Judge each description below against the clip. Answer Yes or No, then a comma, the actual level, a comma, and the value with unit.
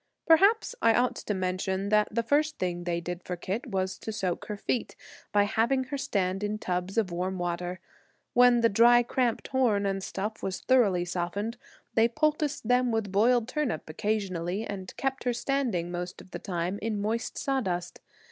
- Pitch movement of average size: Yes, average, 4.7 semitones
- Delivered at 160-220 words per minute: Yes, average, 185 wpm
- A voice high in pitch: Yes, high, 210 Hz